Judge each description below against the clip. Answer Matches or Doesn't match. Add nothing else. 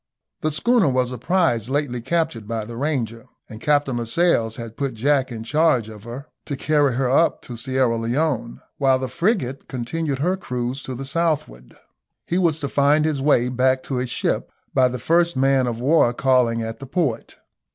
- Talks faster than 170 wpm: Matches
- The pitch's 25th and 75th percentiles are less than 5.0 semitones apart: Matches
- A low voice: Matches